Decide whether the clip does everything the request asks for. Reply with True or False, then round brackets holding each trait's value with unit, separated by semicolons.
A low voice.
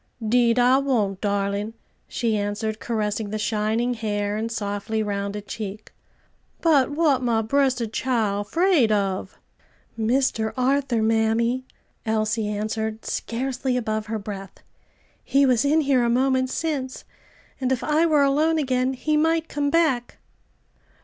False (235 Hz)